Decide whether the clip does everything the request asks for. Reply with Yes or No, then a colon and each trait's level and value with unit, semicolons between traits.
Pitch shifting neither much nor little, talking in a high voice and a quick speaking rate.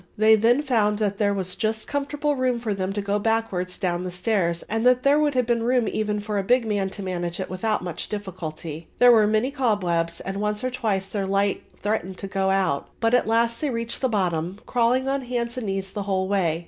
Yes: average, 3.7 semitones; high, 210 Hz; fast, 230 wpm